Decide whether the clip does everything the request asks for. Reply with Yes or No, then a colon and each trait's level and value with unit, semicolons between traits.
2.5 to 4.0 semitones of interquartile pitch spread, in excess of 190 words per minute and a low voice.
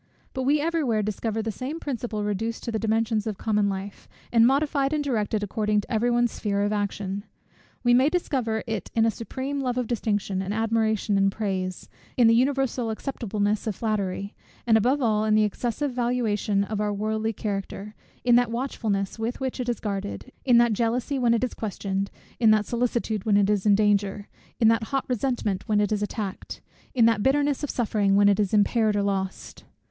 No: average, 2.9 semitones; average, 200 wpm; high, 220 Hz